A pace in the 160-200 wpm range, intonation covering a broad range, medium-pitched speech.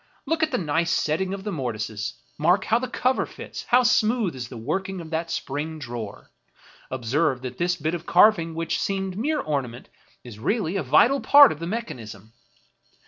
Yes: average, 190 wpm; wide, 7.8 semitones; medium, 165 Hz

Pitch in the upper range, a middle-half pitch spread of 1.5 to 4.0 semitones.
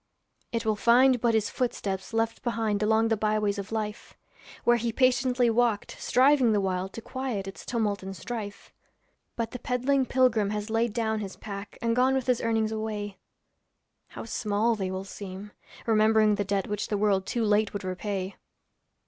Yes: high, 220 Hz; narrow, 2.5 semitones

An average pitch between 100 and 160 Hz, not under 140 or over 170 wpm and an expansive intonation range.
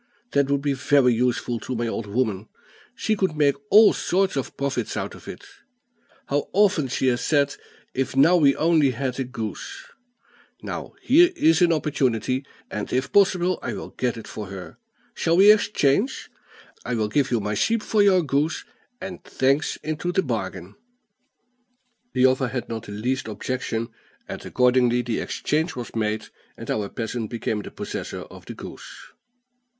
Yes: low, 135 Hz; average, 165 wpm; wide, 5.7 semitones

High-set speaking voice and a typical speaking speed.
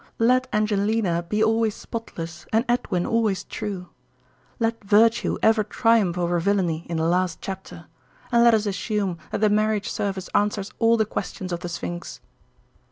Yes: high, 205 Hz; average, 160 wpm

